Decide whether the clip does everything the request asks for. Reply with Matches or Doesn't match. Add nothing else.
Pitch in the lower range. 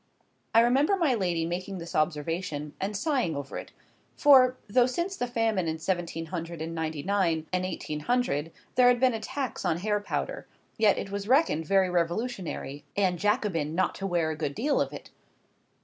Doesn't match